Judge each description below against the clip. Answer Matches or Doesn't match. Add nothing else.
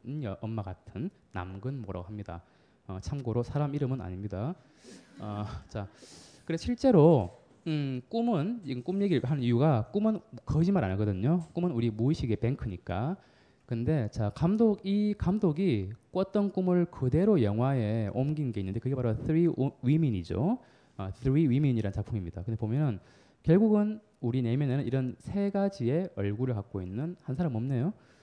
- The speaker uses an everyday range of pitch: Doesn't match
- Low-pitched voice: Matches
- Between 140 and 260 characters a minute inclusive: Doesn't match